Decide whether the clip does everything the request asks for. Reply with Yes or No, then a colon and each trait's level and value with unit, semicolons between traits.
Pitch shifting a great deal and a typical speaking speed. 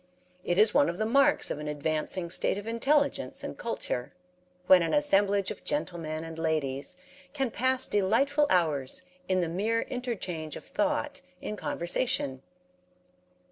Yes: wide, 8.0 semitones; average, 145 wpm